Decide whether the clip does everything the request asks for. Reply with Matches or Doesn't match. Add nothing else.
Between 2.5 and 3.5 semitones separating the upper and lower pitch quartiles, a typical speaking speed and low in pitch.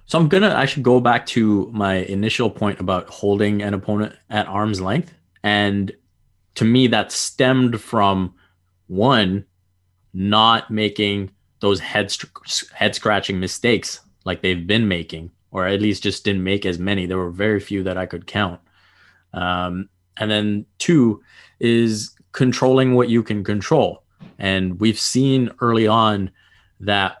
Matches